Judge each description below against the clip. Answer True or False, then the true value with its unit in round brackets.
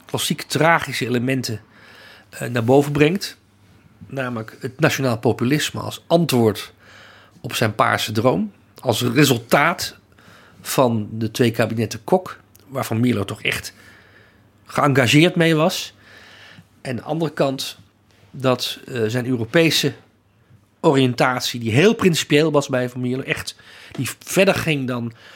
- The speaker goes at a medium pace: False (120 wpm)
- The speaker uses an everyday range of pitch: True (4.8 semitones)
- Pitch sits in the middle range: False (125 Hz)